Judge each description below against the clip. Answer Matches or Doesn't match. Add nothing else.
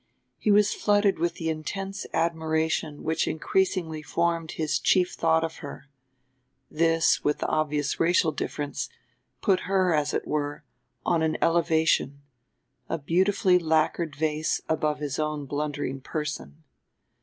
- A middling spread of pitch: Doesn't match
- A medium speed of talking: Doesn't match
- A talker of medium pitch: Matches